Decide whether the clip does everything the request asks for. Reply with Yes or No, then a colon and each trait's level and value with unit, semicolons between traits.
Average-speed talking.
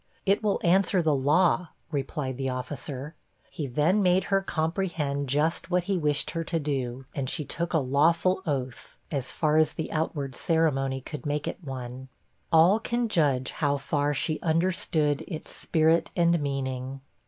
Yes: average, 165 wpm